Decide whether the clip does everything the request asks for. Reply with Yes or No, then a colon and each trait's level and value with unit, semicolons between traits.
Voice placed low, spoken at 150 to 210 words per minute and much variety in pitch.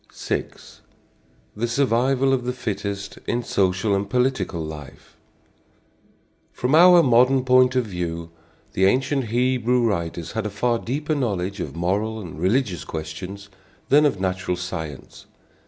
No: low, 105 Hz; slow, 135 wpm; wide, 5.7 semitones